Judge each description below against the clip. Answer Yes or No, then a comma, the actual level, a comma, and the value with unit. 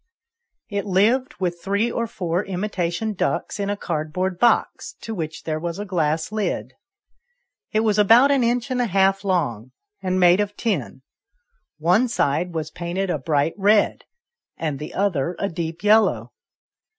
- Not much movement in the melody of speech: No, average, 4.3 semitones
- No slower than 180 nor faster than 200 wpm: No, average, 160 wpm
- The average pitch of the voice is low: No, medium, 185 Hz